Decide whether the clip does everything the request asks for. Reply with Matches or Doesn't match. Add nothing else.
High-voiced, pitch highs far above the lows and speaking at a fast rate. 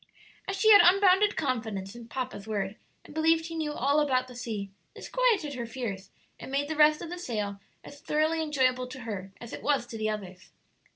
Matches